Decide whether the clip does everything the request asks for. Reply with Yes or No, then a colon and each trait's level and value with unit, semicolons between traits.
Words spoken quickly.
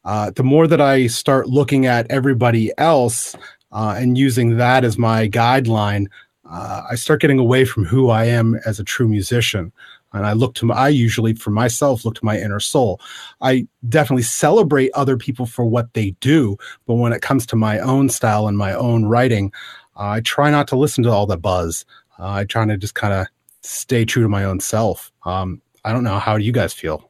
Yes: fast, 210 wpm